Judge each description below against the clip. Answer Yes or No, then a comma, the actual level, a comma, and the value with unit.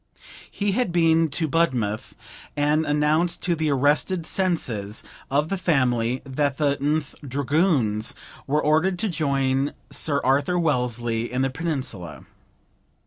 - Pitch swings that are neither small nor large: Yes, average, 4.2 semitones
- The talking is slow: Yes, slow, 130 wpm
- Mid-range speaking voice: Yes, medium, 145 Hz